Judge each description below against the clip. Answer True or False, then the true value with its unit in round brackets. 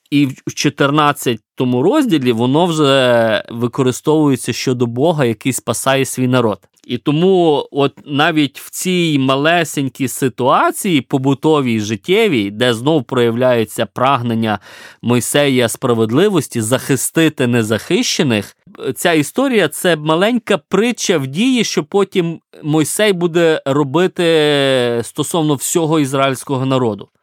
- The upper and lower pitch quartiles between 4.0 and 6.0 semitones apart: True (4.5 semitones)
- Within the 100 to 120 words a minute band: True (105 wpm)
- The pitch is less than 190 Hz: True (140 Hz)